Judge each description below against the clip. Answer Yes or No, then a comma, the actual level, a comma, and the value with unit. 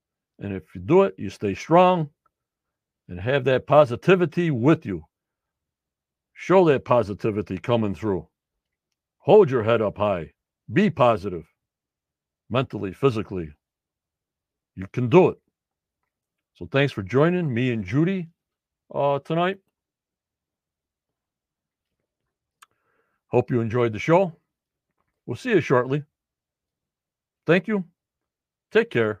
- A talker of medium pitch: No, low, 125 Hz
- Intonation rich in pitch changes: Yes, wide, 8.3 semitones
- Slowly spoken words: Yes, slow, 110 wpm